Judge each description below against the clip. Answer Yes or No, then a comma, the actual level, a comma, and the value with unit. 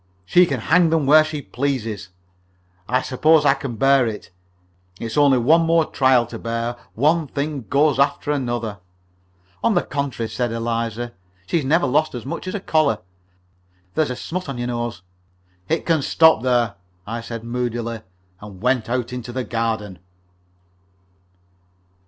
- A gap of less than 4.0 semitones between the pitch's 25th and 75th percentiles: No, average, 4.3 semitones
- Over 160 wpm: No, average, 155 wpm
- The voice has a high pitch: No, low, 125 Hz